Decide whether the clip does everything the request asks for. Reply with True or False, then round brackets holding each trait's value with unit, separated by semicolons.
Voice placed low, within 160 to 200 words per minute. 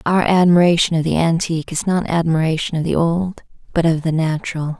False (165 Hz; 190 wpm)